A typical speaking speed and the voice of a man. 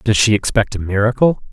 Yes: average, 195 wpm; male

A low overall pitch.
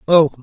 No: medium, 150 Hz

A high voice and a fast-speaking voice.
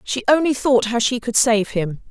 Yes: high, 240 Hz; fast, 230 wpm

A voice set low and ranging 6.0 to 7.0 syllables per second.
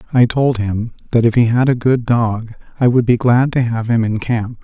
No: low, 115 Hz; 4.9 syllables/s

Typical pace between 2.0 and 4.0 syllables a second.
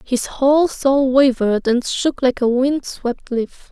Yes: 3.9 syllables/s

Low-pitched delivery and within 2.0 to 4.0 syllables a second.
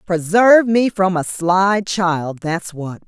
No: medium, 185 Hz; 3.5 syllables/s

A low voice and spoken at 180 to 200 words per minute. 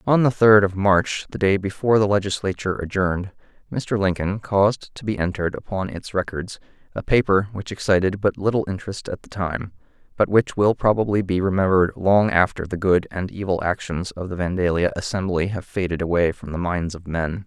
Yes: very low, 95 Hz; average, 190 wpm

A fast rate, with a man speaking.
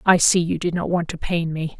No: fast, 300 wpm; female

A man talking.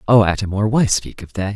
Yes: male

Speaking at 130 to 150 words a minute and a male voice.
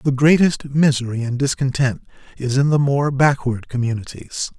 Yes: average, 145 wpm; male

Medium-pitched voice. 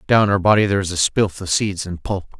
No: very low, 95 Hz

